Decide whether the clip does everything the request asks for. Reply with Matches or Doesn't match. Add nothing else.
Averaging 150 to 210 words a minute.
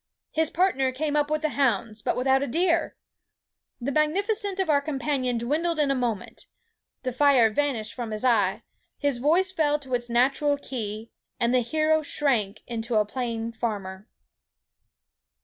Matches